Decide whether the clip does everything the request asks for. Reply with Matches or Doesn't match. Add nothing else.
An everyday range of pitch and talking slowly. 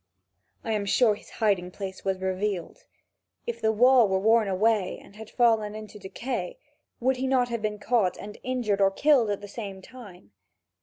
Doesn't match